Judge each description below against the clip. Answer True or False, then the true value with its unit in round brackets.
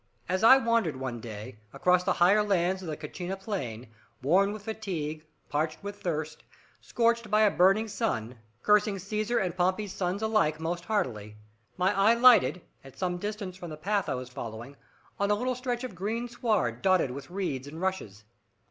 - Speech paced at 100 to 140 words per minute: False (180 wpm)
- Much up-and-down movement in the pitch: True (5.7 semitones)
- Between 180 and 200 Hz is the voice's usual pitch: True (185 Hz)